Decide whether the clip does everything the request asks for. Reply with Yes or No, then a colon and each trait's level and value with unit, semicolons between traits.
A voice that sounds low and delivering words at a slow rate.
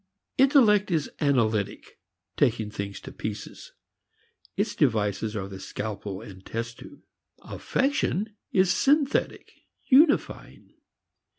Yes: low, 115 Hz; slow, 100 wpm